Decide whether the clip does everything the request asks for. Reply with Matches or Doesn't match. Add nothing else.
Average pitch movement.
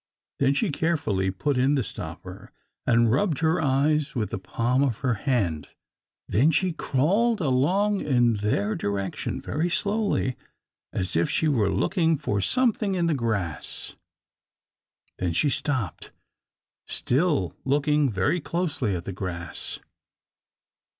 Doesn't match